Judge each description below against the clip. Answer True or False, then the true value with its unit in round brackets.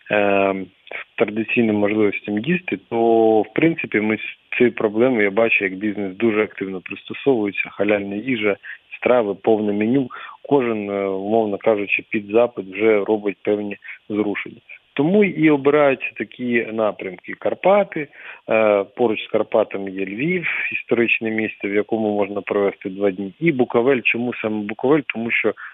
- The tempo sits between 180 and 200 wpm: False (135 wpm)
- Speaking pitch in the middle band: False (110 Hz)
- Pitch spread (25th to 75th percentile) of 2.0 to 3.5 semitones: True (2.8 semitones)